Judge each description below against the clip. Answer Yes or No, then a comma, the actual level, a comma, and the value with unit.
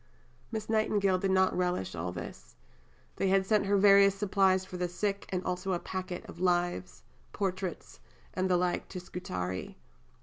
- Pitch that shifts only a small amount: Yes, narrow, 1.7 semitones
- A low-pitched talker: No, medium, 185 Hz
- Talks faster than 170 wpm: No, average, 165 wpm